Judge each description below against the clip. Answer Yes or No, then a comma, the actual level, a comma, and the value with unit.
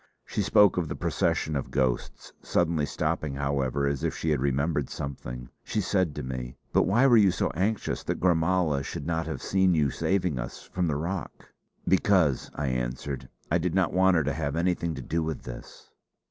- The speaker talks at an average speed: Yes, average, 195 wpm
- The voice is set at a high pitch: No, very low, 80 Hz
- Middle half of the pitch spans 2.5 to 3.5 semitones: No, average, 4.6 semitones